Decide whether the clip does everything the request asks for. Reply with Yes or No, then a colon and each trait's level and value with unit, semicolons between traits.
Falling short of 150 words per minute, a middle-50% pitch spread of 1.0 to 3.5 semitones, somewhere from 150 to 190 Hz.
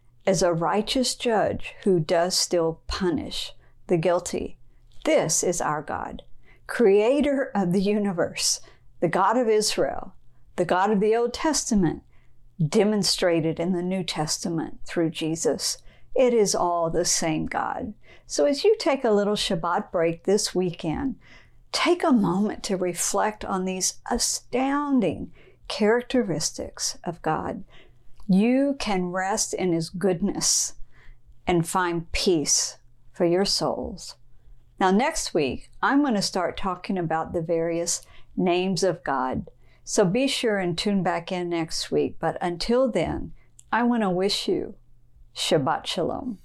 No: average, 140 wpm; average, 4.3 semitones; medium, 185 Hz